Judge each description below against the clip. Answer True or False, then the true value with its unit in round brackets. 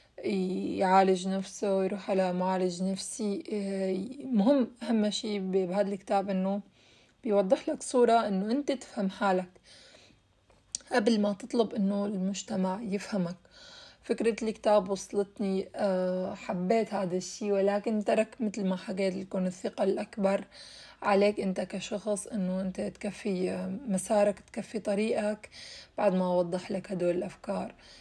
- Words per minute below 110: False (115 wpm)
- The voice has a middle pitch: False (200 Hz)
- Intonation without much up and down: True (1.8 semitones)